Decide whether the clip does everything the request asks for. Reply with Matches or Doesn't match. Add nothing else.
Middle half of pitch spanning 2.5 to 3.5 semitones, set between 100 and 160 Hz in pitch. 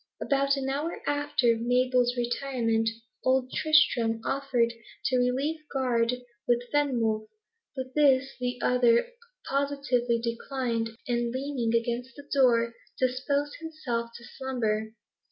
Doesn't match